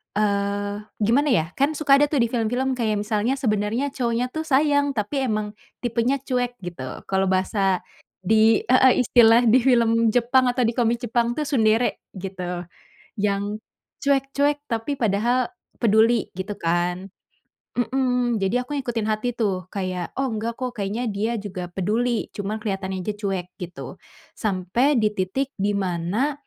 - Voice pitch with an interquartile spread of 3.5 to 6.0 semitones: Yes, average, 3.9 semitones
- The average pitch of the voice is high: Yes, high, 225 Hz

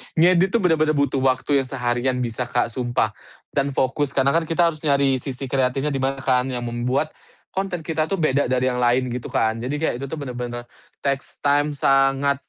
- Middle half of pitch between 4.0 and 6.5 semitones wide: No, average, 2.7 semitones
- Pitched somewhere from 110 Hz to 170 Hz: Yes, low, 135 Hz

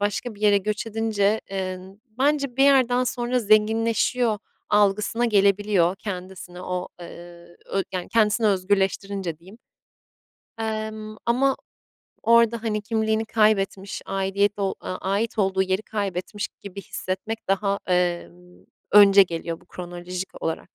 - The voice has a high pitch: Yes, high, 205 Hz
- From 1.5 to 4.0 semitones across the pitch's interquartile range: Yes, average, 2.8 semitones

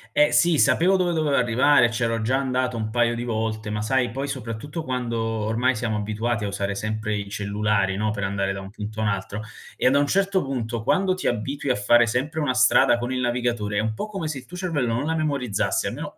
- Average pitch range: Yes, average, 4.4 semitones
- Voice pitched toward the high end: No, low, 120 Hz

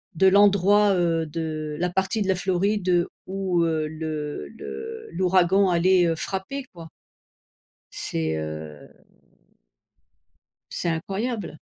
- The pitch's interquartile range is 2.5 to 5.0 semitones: Yes, average, 3.5 semitones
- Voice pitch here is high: No, medium, 180 Hz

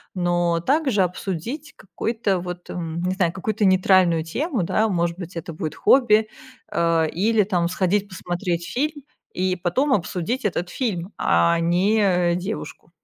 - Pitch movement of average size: Yes, average, 3.8 semitones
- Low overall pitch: No, medium, 185 Hz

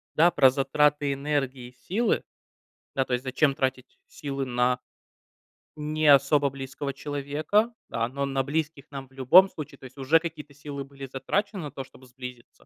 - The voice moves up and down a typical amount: No, narrow, 2.2 semitones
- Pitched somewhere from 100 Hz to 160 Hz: Yes, medium, 140 Hz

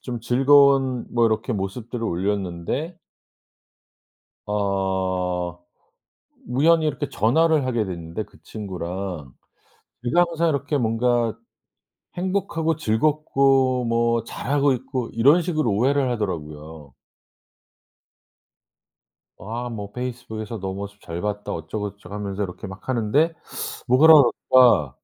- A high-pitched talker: No, low, 115 Hz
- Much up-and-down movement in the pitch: Yes, wide, 5.8 semitones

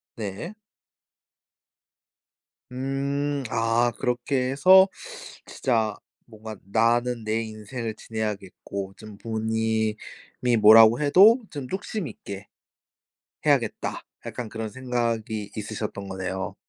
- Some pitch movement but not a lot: Yes, average, 3.0 semitones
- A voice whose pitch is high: No, low, 115 Hz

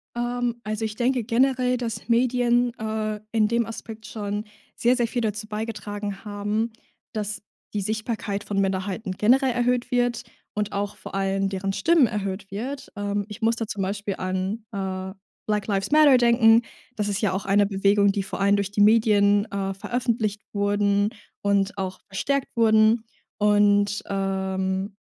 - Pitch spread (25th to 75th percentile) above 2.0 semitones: Yes, narrow, 2.6 semitones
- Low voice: No, high, 210 Hz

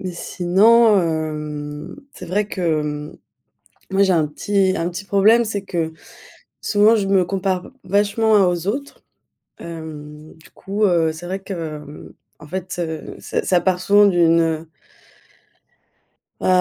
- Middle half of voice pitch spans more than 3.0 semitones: Yes, average, 3.8 semitones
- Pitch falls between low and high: Yes, medium, 180 Hz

